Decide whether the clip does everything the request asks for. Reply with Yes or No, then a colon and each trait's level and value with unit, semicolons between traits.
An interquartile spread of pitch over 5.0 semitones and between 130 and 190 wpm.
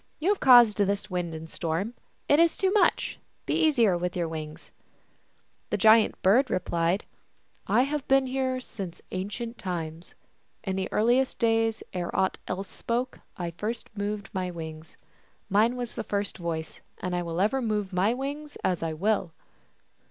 Yes: wide, 5.5 semitones; average, 170 wpm